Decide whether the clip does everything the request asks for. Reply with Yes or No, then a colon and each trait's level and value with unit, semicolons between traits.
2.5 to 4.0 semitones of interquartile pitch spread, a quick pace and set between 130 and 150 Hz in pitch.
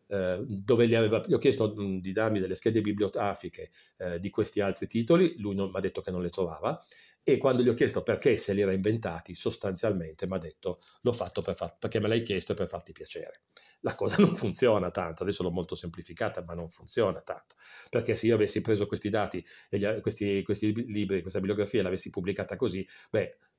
No: average, 2.8 semitones; fast, 200 wpm; low, 105 Hz